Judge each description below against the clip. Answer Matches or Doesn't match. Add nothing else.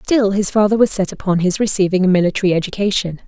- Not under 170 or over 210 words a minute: Matches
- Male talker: Doesn't match